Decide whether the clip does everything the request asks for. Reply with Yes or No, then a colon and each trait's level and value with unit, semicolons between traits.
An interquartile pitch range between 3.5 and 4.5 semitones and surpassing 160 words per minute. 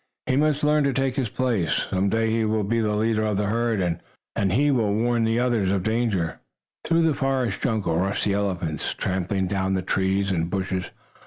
Yes: average, 3.8 semitones; average, 195 wpm